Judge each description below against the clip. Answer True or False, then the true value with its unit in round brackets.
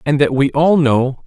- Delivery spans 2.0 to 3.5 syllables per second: False (4.3 syllables/s)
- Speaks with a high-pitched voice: False (140 Hz)